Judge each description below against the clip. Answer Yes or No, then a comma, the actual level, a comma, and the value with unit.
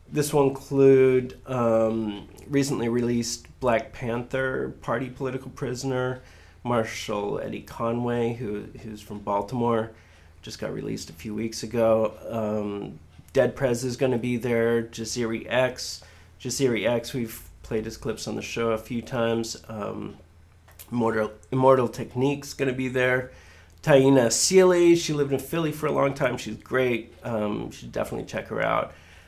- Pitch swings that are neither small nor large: Yes, average, 3.3 semitones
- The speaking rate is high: No, average, 150 wpm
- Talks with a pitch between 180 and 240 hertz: No, low, 115 Hz